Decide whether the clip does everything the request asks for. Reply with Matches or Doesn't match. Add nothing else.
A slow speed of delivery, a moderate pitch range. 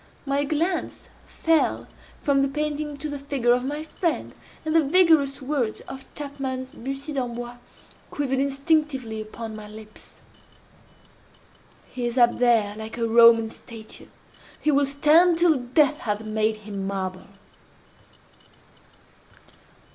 Matches